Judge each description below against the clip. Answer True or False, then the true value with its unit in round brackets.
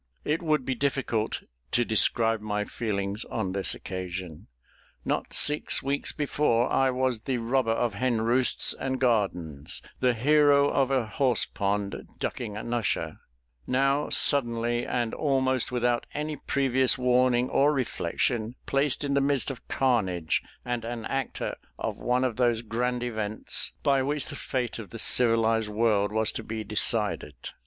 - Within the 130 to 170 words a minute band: True (150 wpm)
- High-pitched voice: False (120 Hz)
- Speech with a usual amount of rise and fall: True (3.3 semitones)